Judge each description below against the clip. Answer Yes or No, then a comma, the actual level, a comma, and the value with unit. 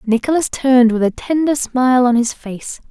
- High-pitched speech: Yes, very high, 250 Hz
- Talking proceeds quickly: No, average, 185 wpm